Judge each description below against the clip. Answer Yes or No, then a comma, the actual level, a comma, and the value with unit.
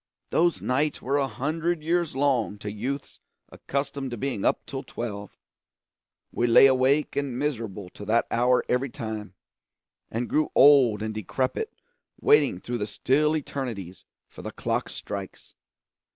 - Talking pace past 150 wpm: No, average, 145 wpm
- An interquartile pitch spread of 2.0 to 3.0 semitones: No, average, 4.6 semitones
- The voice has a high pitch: No, low, 130 Hz